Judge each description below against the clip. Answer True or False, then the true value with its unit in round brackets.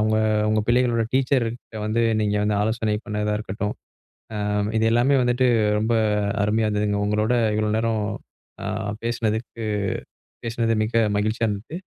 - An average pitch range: False (1.8 semitones)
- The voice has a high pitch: False (110 Hz)